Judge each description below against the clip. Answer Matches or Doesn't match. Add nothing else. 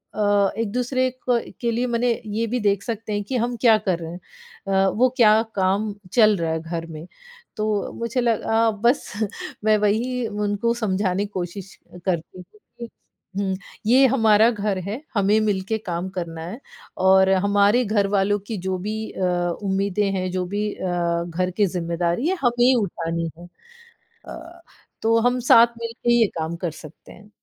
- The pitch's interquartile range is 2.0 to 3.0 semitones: Doesn't match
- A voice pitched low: Doesn't match